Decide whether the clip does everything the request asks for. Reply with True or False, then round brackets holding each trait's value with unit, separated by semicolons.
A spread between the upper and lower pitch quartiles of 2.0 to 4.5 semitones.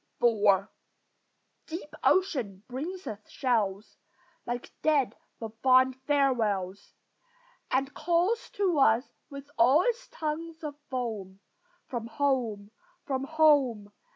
False (5.6 semitones)